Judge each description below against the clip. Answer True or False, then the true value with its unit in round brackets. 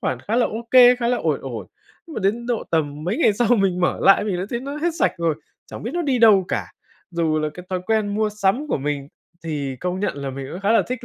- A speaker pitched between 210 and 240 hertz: False (200 Hz)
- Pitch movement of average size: False (6.3 semitones)